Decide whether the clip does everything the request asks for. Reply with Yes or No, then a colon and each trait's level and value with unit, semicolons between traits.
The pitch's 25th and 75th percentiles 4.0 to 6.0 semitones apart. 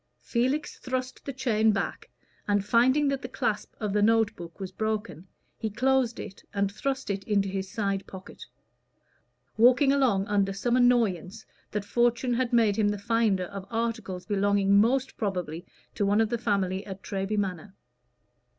No: average, 3.4 semitones